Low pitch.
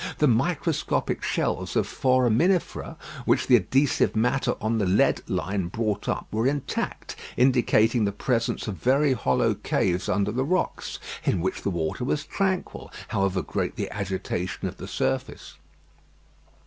Yes: low, 115 Hz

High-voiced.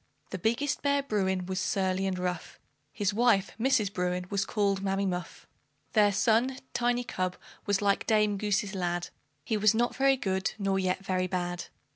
Yes: high, 195 Hz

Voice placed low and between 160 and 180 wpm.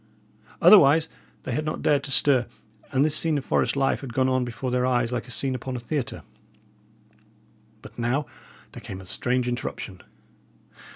Yes: low, 130 Hz; average, 175 wpm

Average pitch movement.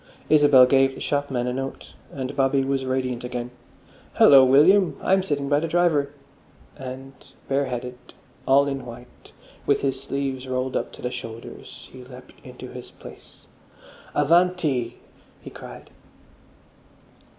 No: narrow, 1.9 semitones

